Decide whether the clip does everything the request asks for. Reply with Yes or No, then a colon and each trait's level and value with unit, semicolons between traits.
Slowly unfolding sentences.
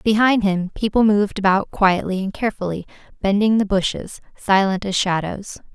No: average, 145 wpm